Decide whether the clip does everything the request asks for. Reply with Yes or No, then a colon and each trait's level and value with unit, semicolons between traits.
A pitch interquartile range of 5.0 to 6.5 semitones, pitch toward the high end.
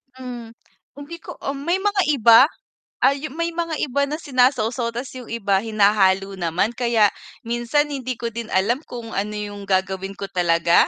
Yes: wide, 5.5 semitones; high, 235 Hz